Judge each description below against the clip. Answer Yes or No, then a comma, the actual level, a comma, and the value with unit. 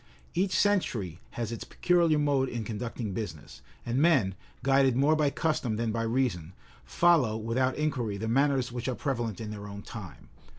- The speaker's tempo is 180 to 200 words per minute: No, average, 170 wpm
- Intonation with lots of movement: No, average, 4.5 semitones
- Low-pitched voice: Yes, low, 120 Hz